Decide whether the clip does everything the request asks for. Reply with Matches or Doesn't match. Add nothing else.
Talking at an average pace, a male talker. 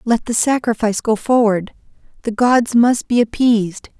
Doesn't match